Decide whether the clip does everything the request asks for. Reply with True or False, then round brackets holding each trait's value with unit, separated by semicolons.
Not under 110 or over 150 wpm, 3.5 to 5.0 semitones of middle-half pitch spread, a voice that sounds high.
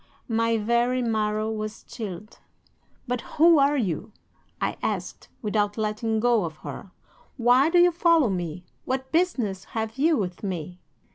True (145 wpm; 4.0 semitones; 225 Hz)